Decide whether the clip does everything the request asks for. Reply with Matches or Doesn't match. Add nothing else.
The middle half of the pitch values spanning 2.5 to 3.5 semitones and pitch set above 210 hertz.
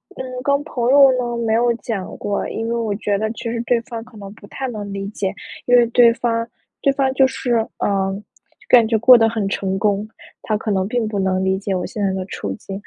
Matches